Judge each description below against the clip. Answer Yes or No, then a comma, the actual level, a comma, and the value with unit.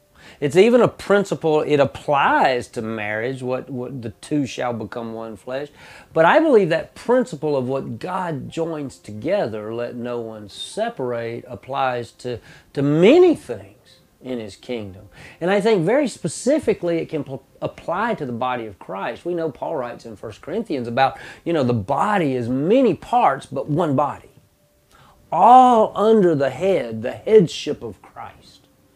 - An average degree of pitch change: No, wide, 6.4 semitones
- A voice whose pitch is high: No, low, 135 Hz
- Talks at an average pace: Yes, average, 160 wpm